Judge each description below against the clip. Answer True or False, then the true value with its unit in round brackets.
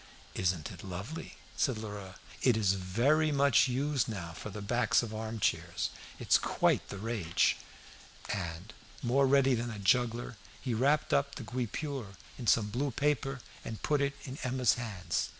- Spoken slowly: False (165 wpm)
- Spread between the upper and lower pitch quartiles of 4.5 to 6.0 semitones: True (5.0 semitones)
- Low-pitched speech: True (120 Hz)